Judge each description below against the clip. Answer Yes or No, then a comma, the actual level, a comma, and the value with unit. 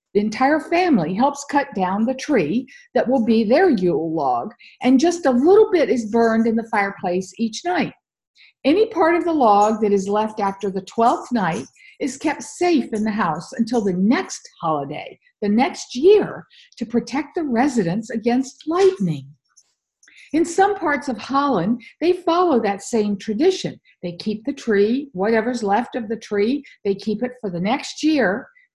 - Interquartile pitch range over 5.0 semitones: Yes, wide, 5.6 semitones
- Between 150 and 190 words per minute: Yes, average, 175 wpm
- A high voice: Yes, high, 240 Hz